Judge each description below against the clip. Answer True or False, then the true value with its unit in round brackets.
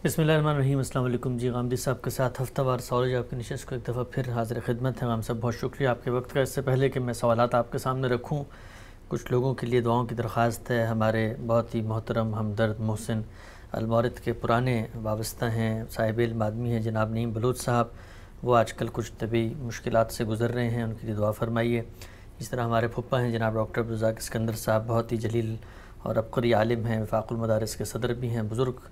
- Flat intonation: True (1.9 semitones)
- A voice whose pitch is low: True (115 Hz)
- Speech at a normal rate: False (220 wpm)